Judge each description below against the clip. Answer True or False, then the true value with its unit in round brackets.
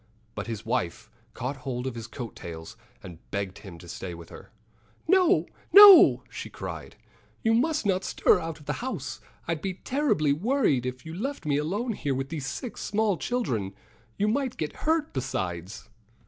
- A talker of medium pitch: True (150 Hz)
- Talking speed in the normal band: True (180 wpm)